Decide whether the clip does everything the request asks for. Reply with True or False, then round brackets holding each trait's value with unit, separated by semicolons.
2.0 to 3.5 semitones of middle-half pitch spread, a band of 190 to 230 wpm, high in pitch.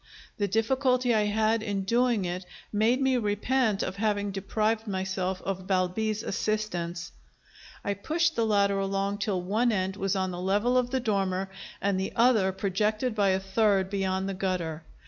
False (2.6 semitones; 165 wpm; 200 Hz)